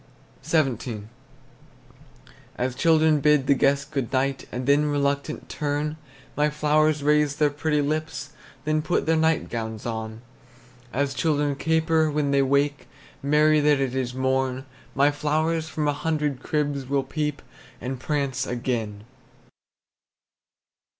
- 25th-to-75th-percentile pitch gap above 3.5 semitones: No, narrow, 2.4 semitones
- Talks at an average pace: No, slow, 130 wpm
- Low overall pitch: No, medium, 145 Hz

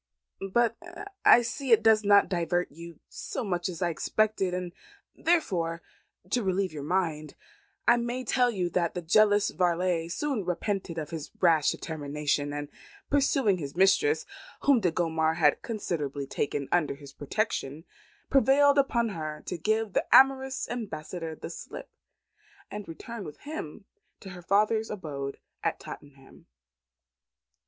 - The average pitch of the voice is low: No, medium, 180 Hz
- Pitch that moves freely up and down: Yes, wide, 5.8 semitones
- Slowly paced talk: No, average, 145 wpm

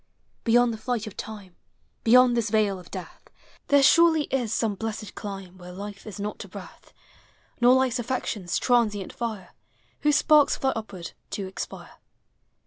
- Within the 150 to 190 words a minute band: Yes, average, 160 wpm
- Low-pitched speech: No, high, 220 Hz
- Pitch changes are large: No, average, 3.8 semitones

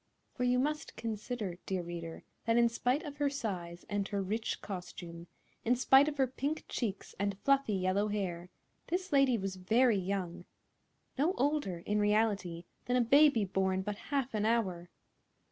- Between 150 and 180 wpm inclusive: Yes, average, 160 wpm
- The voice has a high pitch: Yes, high, 210 Hz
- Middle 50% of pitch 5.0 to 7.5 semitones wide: Yes, wide, 5.5 semitones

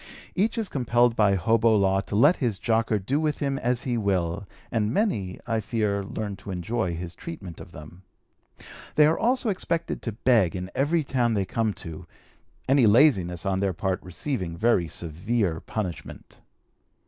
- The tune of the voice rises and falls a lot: No, average, 5.0 semitones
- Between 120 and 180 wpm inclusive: Yes, average, 170 wpm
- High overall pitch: No, low, 110 Hz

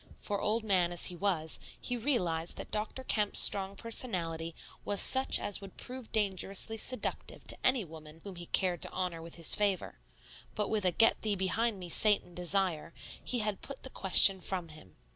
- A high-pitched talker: Yes, high, 195 Hz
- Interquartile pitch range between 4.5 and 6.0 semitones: No, average, 3.8 semitones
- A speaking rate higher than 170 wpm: Yes, average, 185 wpm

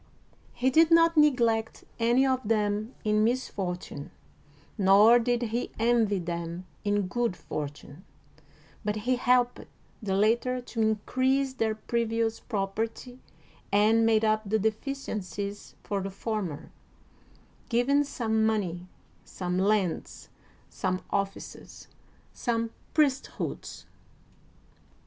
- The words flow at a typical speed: No, slow, 110 wpm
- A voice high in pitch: Yes, high, 220 Hz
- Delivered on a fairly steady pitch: No, average, 3.4 semitones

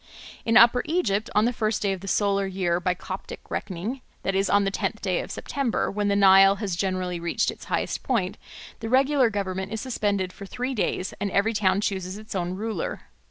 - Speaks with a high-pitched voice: Yes, high, 200 Hz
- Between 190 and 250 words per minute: Yes, fast, 205 wpm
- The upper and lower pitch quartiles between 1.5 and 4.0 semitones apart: Yes, average, 2.8 semitones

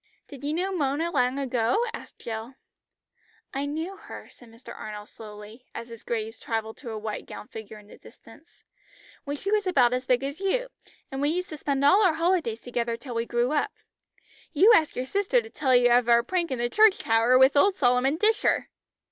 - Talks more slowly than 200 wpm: No, fast, 205 wpm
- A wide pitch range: Yes, wide, 5.9 semitones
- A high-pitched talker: Yes, very high, 265 Hz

